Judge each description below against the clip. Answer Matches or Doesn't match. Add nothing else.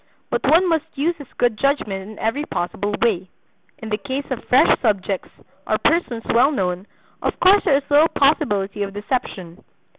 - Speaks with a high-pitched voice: Matches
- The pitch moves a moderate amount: Doesn't match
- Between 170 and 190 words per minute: Matches